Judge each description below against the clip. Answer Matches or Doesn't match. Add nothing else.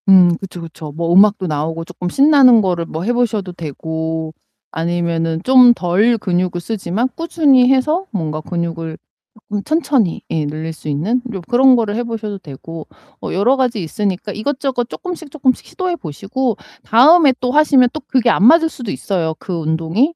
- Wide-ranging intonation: Matches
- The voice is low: Doesn't match